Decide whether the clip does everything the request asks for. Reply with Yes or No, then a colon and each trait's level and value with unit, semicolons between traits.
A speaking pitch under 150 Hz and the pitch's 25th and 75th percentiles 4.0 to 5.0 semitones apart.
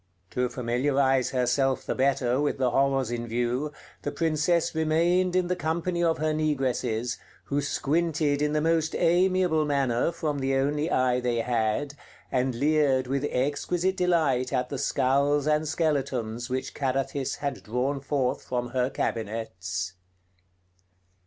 No: medium, 140 Hz; average, 3.6 semitones